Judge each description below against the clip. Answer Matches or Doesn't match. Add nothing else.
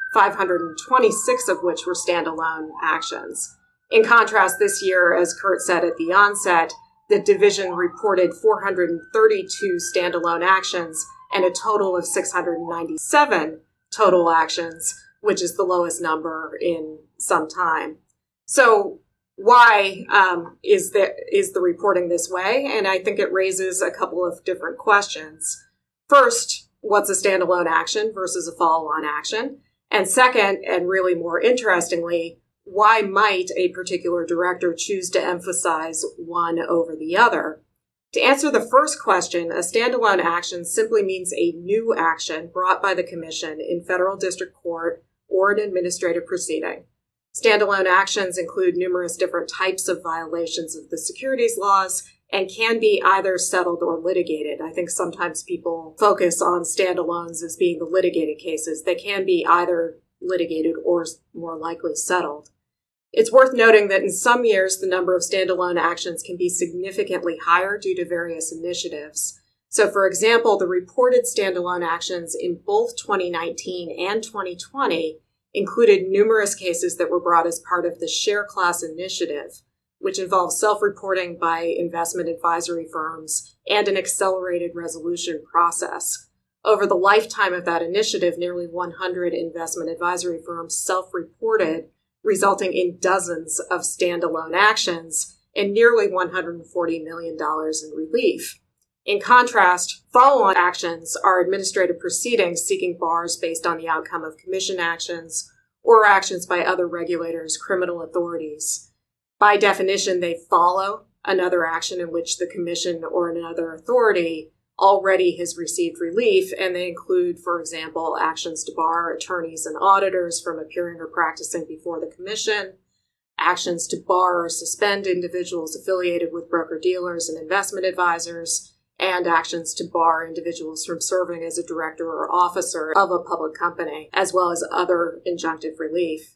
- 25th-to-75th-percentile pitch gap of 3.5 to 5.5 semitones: Doesn't match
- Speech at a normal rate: Matches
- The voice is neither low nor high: Matches